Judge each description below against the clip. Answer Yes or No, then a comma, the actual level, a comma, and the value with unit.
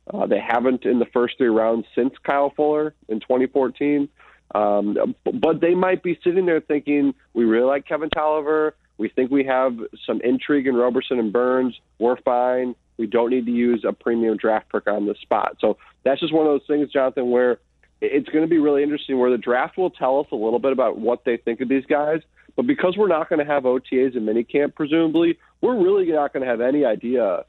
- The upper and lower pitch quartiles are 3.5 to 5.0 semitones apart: Yes, average, 4.0 semitones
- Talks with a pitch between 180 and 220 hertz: No, low, 135 Hz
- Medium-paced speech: No, fast, 220 wpm